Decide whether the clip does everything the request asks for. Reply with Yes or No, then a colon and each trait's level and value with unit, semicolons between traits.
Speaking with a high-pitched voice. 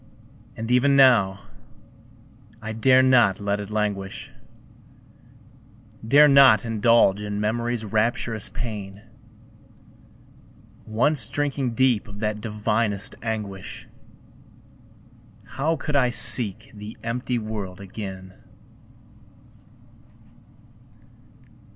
No: low, 110 Hz